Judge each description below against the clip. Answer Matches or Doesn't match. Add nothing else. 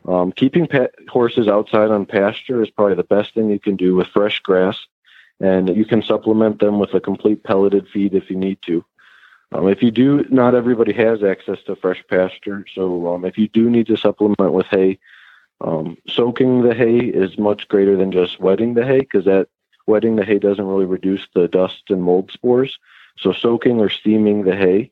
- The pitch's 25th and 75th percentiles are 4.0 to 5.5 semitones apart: Doesn't match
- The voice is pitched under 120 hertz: Matches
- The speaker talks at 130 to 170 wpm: Doesn't match